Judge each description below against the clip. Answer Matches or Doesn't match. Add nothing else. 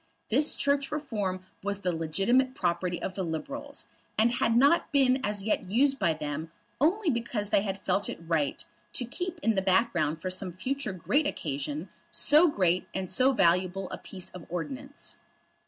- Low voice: Doesn't match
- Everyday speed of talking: Matches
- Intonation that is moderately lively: Doesn't match